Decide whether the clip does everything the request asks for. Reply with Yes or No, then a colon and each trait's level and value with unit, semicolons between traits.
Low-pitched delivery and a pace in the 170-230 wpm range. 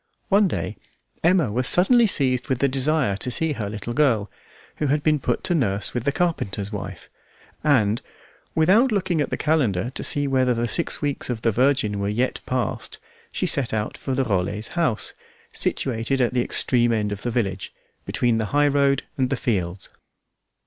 Yes: low, 125 Hz; average, 185 wpm